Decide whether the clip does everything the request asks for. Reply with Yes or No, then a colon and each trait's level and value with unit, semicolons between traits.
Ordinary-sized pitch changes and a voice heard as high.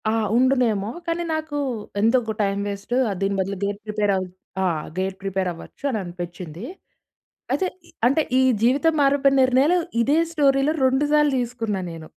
No: wide, 5.9 semitones; high, 230 Hz